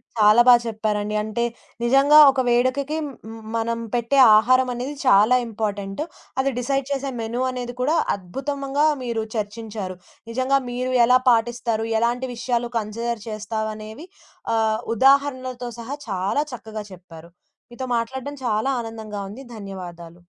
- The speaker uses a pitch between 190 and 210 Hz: No, high, 235 Hz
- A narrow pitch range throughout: No, average, 3.2 semitones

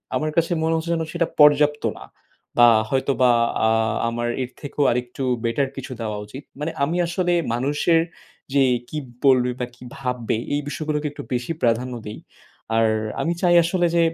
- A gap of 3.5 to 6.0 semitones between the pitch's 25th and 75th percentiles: Yes, average, 4.5 semitones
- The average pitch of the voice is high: No, medium, 140 Hz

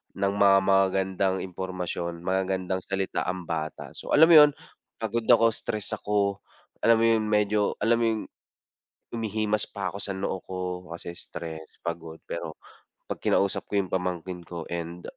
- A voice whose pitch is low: Yes, very low, 95 Hz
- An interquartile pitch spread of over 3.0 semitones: No, average, 2.7 semitones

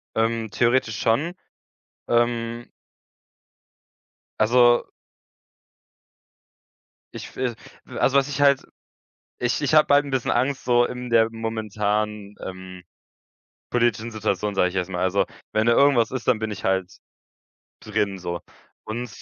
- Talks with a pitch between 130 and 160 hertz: No, low, 115 Hz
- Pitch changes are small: No, average, 3.0 semitones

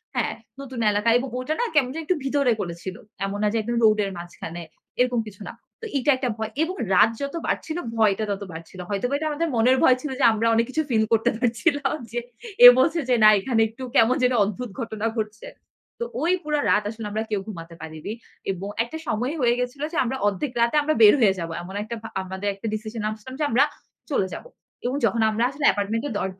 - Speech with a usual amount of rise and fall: Yes, average, 4.1 semitones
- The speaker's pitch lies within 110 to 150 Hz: No, high, 230 Hz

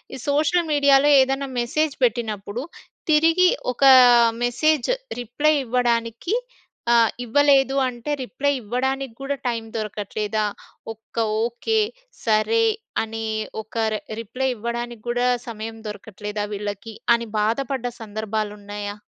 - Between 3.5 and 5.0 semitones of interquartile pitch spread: Yes, average, 4.0 semitones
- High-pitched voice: Yes, high, 235 Hz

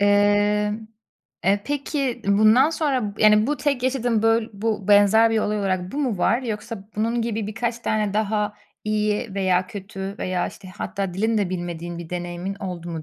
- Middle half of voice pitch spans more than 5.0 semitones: No, average, 2.7 semitones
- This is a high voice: Yes, high, 210 Hz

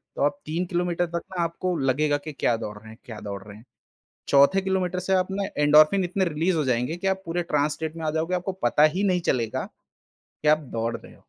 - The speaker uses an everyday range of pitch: Yes, average, 4.7 semitones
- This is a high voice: No, medium, 160 Hz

